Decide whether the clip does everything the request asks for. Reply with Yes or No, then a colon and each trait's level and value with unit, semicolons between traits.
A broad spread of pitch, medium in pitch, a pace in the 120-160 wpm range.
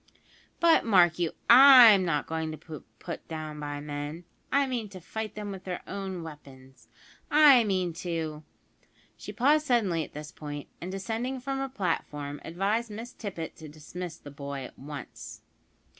No: wide, 6.7 semitones; medium, 175 Hz; average, 170 wpm